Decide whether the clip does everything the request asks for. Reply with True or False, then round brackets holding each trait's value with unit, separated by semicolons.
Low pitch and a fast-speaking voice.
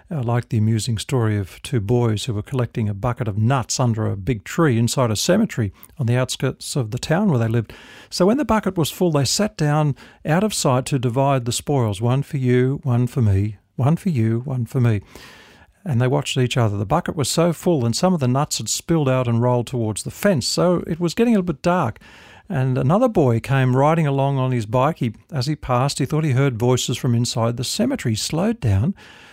True (130 Hz; 235 wpm)